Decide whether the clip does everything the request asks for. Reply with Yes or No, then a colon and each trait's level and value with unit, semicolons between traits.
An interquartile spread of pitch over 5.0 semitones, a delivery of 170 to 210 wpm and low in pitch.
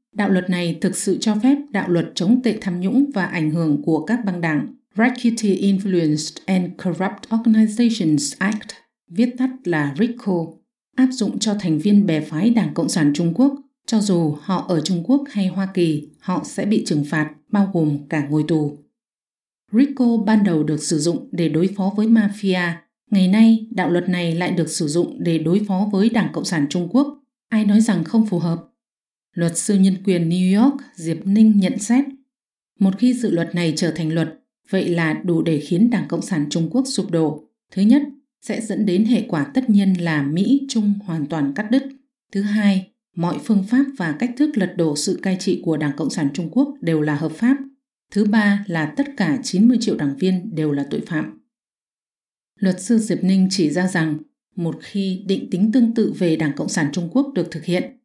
No: wide, 5.4 semitones; fast, 205 wpm; high, 190 Hz